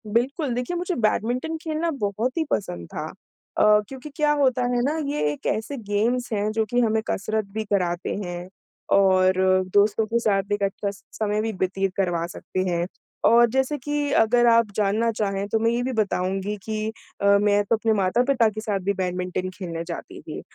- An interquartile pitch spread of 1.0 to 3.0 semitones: No, average, 3.7 semitones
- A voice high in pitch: Yes, high, 215 Hz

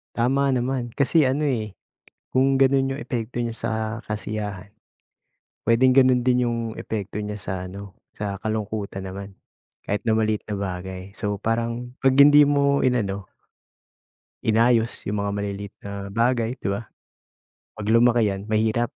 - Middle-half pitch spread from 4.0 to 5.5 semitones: No, average, 3.6 semitones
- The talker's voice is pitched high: No, low, 115 Hz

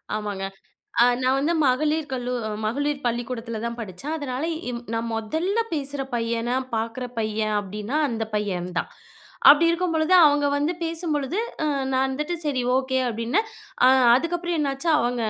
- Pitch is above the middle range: Yes, very high, 260 Hz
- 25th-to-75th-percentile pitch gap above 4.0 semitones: Yes, average, 4.7 semitones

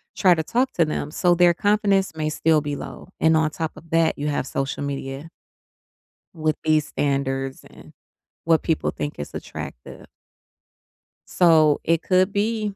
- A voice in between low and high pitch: Yes, medium, 160 Hz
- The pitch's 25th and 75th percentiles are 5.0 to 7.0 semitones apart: No, average, 3.3 semitones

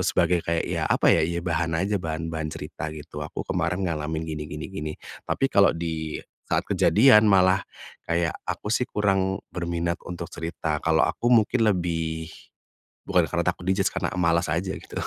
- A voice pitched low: Yes, very low, 85 Hz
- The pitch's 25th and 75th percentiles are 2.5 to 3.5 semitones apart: Yes, average, 2.8 semitones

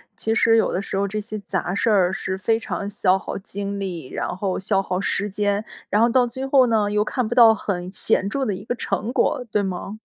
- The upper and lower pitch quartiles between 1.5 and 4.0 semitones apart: Yes, average, 2.7 semitones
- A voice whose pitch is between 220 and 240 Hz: No, high, 205 Hz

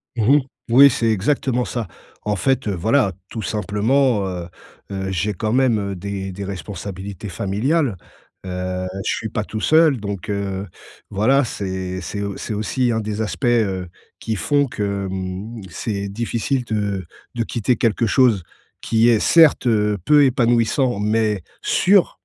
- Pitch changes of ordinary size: Yes, average, 3.5 semitones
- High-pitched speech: No, low, 105 Hz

